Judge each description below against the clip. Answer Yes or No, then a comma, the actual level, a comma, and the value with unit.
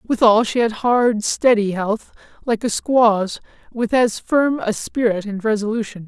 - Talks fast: No, average, 160 wpm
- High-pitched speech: Yes, high, 225 Hz